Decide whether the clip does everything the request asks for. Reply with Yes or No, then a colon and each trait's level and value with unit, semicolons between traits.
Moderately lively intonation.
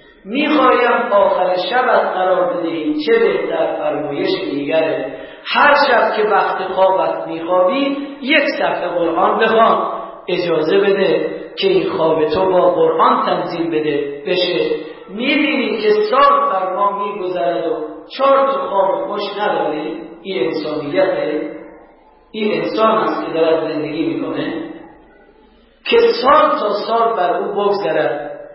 No: wide, 7.1 semitones